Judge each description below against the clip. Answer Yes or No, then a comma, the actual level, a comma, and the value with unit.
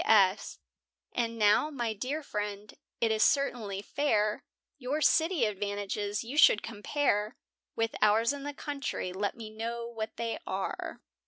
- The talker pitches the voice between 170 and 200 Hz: No, high, 225 Hz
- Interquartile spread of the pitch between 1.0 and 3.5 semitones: No, average, 4.5 semitones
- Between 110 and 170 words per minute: Yes, average, 145 wpm